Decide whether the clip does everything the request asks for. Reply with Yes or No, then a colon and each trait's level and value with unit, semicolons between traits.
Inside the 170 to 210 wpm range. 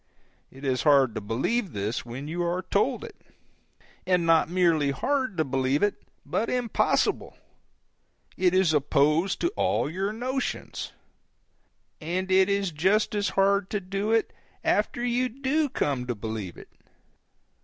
No: average, 145 wpm